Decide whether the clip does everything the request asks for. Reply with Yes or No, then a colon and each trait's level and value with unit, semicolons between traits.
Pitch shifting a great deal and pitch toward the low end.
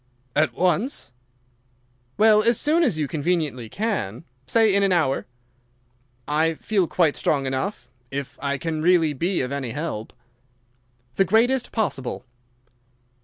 No: wide, 6.6 semitones; medium, 165 Hz